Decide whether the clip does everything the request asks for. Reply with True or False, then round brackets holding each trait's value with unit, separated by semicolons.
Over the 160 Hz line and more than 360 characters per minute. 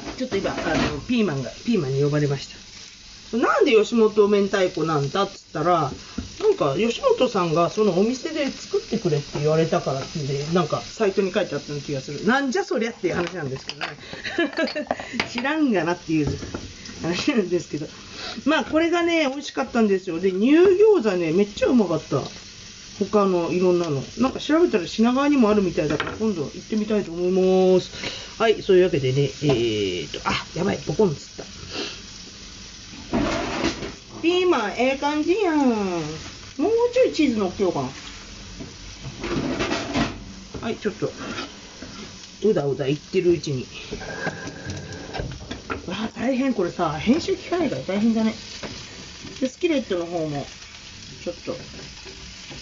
False (190 Hz; 330 characters per minute)